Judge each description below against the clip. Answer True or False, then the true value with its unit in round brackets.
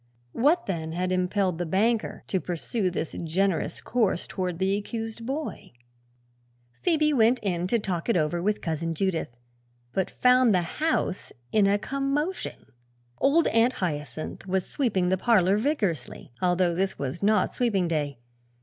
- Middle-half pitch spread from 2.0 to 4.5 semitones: False (5.0 semitones)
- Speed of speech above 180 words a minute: False (150 wpm)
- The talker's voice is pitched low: False (190 Hz)